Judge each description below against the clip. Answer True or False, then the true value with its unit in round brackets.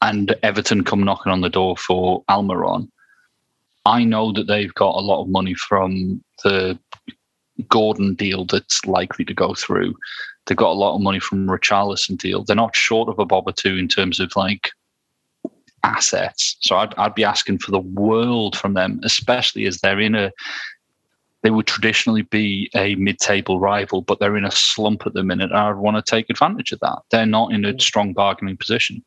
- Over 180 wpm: True (195 wpm)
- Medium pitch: False (100 Hz)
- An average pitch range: False (2.1 semitones)